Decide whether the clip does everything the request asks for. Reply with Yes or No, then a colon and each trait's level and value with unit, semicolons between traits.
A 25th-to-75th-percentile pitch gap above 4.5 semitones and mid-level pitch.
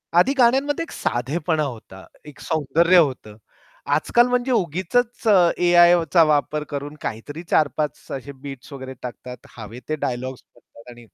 Yes: wide, 5.4 semitones; medium, 150 Hz